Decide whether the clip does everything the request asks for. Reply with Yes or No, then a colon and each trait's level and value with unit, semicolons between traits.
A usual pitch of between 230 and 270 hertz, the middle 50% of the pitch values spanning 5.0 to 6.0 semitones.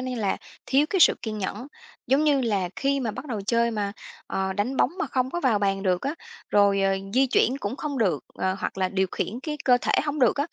Yes: high, 235 Hz; wide, 5.4 semitones